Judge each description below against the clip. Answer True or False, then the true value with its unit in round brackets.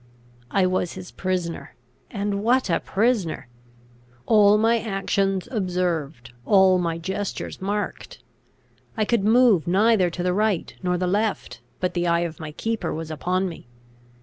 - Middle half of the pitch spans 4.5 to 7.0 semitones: False (3.3 semitones)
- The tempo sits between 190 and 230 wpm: False (150 wpm)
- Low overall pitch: False (185 Hz)